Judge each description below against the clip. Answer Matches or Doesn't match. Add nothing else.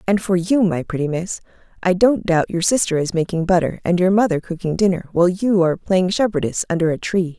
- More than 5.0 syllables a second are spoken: Matches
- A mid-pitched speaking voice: Matches